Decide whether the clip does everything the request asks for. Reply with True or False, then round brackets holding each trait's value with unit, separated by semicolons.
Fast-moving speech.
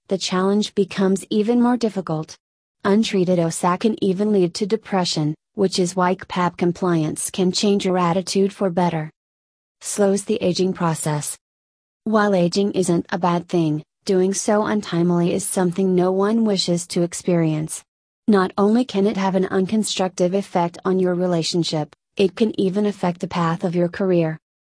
False (155 wpm)